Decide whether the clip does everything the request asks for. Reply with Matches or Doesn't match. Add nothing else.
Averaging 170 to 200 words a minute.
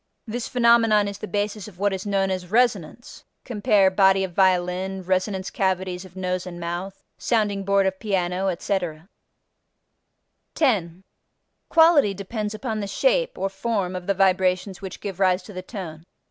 Doesn't match